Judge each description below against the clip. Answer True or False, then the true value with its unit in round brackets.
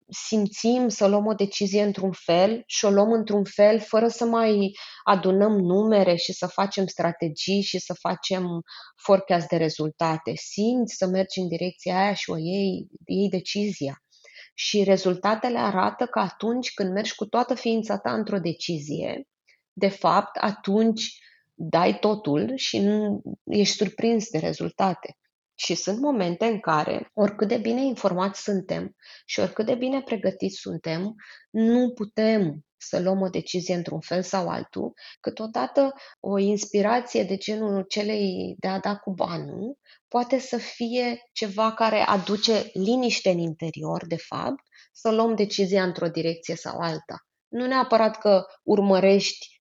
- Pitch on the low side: False (200 Hz)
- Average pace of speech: True (145 wpm)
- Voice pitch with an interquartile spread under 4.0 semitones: True (3.3 semitones)